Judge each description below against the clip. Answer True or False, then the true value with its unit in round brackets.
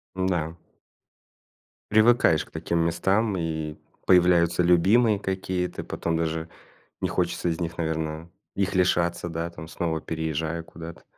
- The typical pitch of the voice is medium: False (85 Hz)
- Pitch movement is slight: True (2.2 semitones)